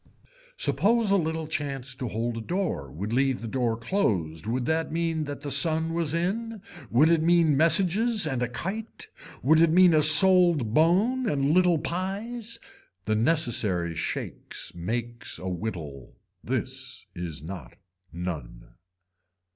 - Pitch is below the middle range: No, medium, 150 Hz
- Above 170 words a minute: No, average, 145 wpm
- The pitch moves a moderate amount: No, wide, 7.6 semitones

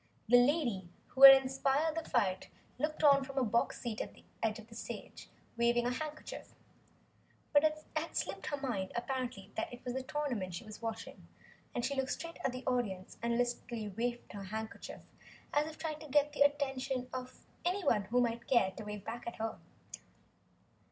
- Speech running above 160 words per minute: Yes, average, 190 wpm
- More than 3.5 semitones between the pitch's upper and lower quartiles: Yes, average, 4.0 semitones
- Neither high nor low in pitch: No, high, 245 Hz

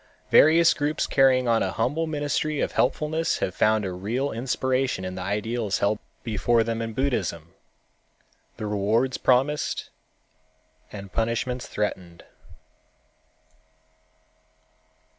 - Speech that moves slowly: Yes, slow, 110 wpm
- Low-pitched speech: Yes, low, 115 Hz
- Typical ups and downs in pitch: Yes, average, 4.6 semitones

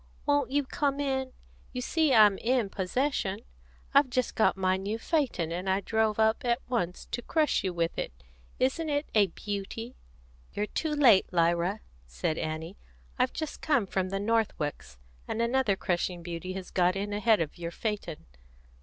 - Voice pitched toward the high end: Yes, high, 210 Hz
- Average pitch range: No, wide, 5.8 semitones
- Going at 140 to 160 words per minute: No, average, 170 wpm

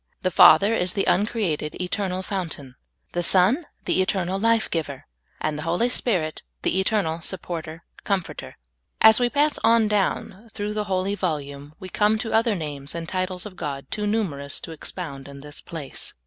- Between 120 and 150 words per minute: No, average, 175 wpm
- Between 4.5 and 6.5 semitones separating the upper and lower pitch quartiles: Yes, average, 4.9 semitones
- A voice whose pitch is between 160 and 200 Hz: Yes, medium, 185 Hz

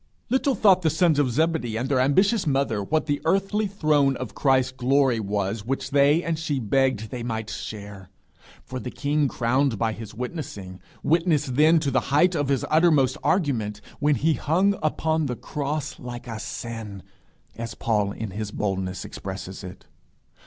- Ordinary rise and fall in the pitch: No, wide, 5.7 semitones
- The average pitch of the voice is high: No, low, 135 Hz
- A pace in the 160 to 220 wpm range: Yes, average, 170 wpm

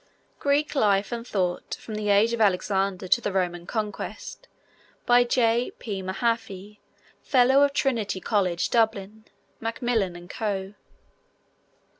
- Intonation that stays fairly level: No, average, 3.6 semitones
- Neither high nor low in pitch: No, high, 210 Hz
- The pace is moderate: No, slow, 125 wpm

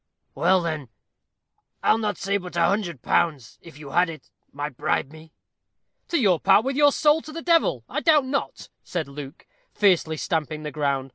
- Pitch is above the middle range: No, medium, 170 Hz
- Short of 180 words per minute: No, average, 185 wpm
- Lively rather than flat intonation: Yes, wide, 5.9 semitones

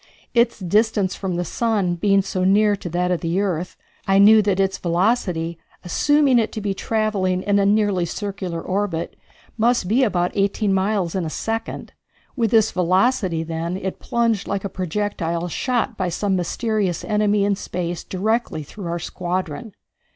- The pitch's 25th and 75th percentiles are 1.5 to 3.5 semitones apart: Yes, average, 3.2 semitones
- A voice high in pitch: Yes, high, 195 Hz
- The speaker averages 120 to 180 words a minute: Yes, average, 165 wpm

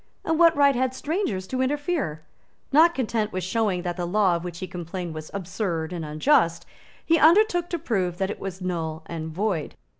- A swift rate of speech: No, average, 190 wpm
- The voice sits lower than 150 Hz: No, high, 190 Hz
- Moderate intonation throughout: No, wide, 8.4 semitones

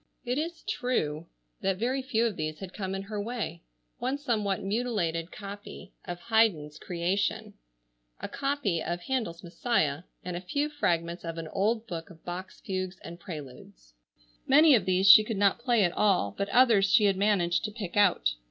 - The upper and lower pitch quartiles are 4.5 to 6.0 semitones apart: Yes, average, 5.1 semitones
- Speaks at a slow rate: No, average, 180 wpm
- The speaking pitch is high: Yes, high, 195 Hz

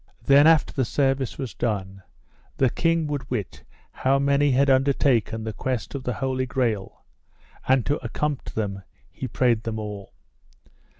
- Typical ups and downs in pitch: Yes, average, 3.8 semitones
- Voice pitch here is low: Yes, low, 130 Hz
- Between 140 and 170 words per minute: Yes, average, 155 wpm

